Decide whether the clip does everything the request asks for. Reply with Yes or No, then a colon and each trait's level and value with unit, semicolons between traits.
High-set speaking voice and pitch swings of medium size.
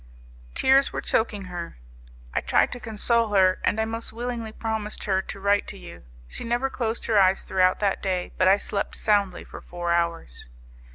Yes: high, 205 Hz; average, 3.4 semitones